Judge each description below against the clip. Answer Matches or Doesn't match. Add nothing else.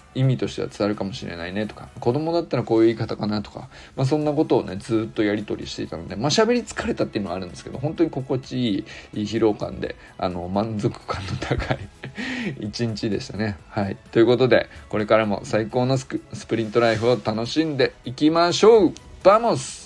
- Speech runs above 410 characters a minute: Matches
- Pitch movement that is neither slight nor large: Matches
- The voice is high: Doesn't match